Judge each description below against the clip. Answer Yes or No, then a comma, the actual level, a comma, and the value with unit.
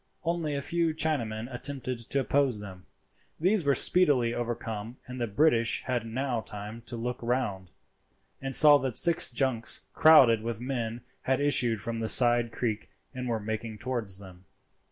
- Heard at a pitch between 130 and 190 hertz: No, low, 120 Hz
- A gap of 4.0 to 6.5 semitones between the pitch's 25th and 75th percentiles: No, average, 3.5 semitones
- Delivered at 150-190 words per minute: Yes, average, 160 wpm